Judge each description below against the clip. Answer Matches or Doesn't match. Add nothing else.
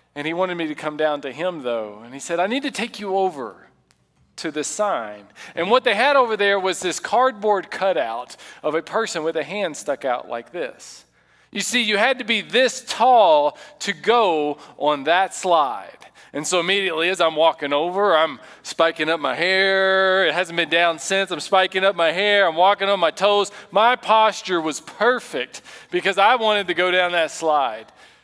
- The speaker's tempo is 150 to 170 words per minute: Doesn't match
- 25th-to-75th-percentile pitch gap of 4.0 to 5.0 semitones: Matches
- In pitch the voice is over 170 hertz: Matches